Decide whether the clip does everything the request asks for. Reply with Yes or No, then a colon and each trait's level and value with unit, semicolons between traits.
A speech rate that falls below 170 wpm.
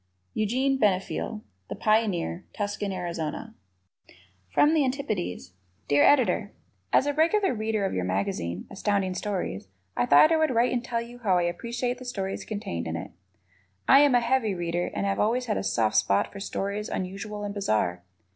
No: average, 175 wpm